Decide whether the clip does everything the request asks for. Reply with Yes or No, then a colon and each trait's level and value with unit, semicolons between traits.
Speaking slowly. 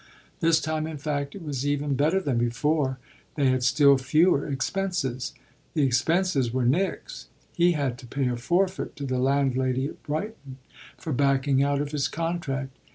No: average, 165 wpm